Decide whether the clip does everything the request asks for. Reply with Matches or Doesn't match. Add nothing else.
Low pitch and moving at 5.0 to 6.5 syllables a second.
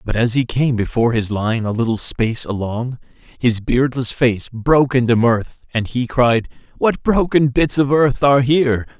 Doesn't match